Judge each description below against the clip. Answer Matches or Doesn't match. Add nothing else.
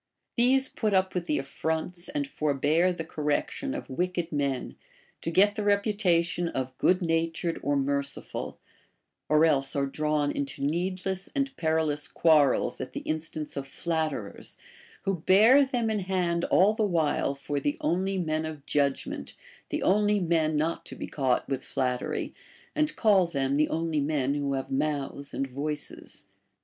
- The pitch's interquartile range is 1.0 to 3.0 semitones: Doesn't match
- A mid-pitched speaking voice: Matches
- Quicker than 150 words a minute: Matches